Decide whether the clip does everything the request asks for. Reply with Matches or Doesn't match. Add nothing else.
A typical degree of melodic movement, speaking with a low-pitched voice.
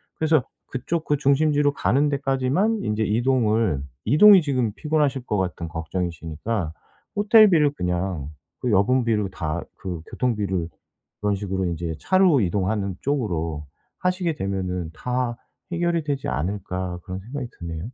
Doesn't match